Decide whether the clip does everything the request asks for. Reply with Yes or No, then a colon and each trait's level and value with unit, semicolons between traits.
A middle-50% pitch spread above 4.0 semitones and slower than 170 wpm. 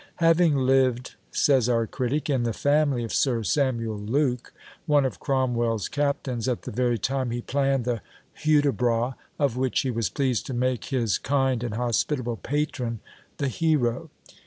No: average, 3.1 semitones; average, 160 wpm